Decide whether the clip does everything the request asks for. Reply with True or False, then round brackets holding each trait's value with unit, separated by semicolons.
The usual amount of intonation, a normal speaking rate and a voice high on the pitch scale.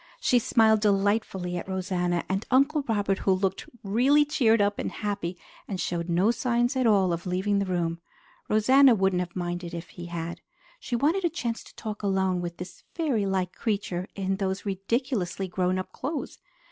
True (4.1 semitones; 185 wpm; 195 Hz)